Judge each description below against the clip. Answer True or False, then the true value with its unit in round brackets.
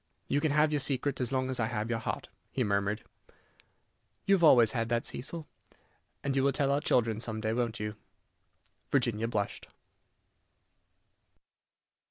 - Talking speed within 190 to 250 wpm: False (160 wpm)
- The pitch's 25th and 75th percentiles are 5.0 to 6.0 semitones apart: False (3.9 semitones)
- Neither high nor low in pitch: False (120 Hz)